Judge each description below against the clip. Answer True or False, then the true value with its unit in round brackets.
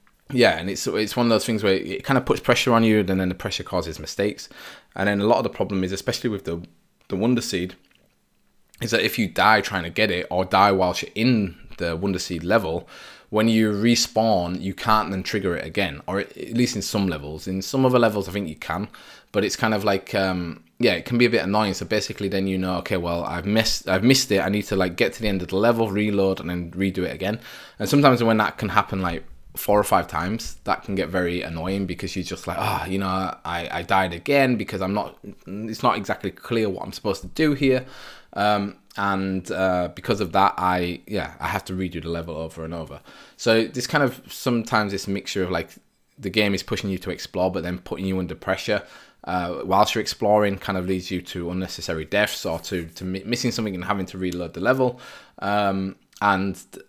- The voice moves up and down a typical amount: True (3.0 semitones)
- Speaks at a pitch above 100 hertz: False (95 Hz)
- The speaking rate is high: True (240 wpm)